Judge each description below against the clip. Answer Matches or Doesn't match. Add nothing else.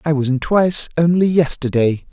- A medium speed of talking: Matches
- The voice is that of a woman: Doesn't match